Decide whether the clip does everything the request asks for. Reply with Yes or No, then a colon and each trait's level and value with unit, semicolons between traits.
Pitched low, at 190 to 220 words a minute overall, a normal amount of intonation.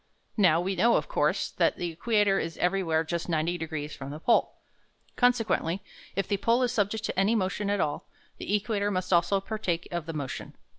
No: high, 190 Hz; average, 195 wpm; average, 4.0 semitones